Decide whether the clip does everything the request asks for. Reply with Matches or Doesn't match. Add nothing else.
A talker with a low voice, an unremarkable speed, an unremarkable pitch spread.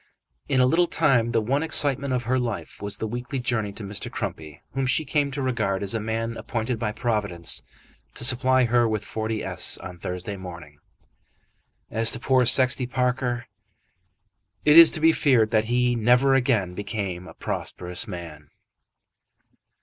Matches